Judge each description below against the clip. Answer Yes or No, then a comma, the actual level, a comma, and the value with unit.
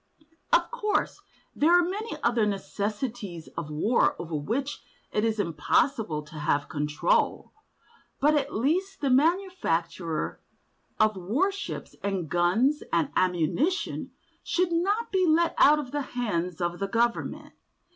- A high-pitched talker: Yes, high, 230 Hz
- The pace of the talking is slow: Yes, slow, 130 wpm